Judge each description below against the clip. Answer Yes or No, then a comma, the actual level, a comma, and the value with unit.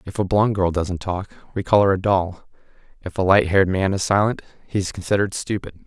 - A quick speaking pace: Yes, fast, 215 wpm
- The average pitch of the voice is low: Yes, very low, 95 Hz